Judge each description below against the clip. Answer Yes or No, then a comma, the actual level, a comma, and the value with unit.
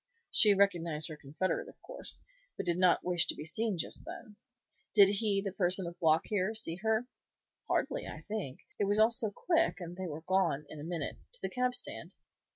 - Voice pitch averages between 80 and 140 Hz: No, high, 190 Hz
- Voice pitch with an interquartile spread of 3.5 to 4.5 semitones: Yes, average, 4.1 semitones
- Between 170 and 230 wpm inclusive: Yes, fast, 205 wpm